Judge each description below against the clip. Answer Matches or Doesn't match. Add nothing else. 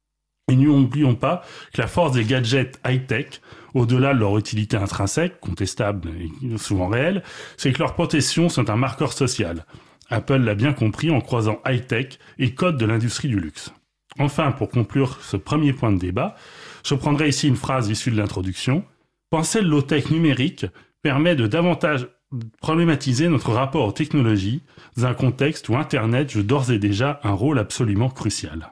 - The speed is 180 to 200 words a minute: Doesn't match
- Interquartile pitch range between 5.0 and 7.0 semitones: Matches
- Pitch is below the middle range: Matches